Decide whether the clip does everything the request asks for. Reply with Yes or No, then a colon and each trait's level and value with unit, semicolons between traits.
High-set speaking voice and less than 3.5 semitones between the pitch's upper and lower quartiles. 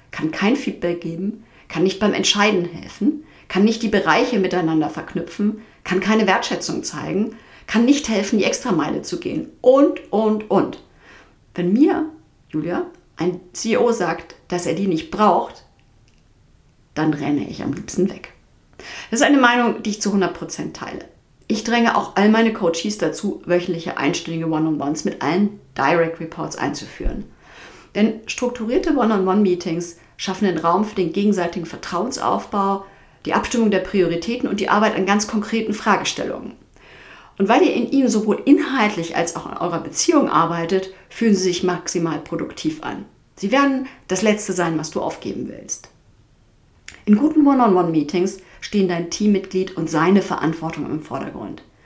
No: high, 195 Hz; average, 4.4 semitones